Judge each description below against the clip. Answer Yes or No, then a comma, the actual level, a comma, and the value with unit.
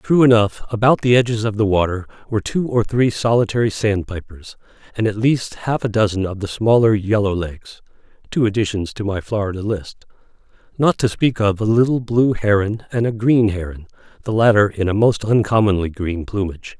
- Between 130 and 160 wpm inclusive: No, average, 170 wpm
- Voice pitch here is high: No, low, 105 Hz